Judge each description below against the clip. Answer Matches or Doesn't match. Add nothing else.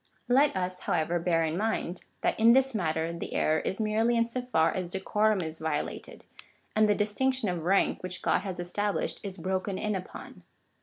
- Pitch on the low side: Doesn't match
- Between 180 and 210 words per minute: Matches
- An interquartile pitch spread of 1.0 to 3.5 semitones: Doesn't match